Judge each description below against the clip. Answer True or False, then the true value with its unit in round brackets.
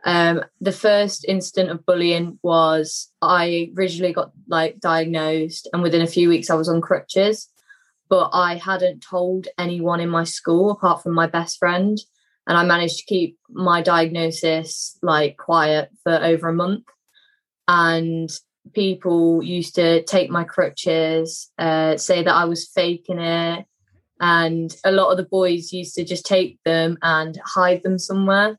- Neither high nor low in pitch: True (170 Hz)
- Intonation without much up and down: True (2.1 semitones)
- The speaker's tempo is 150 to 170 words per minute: True (160 wpm)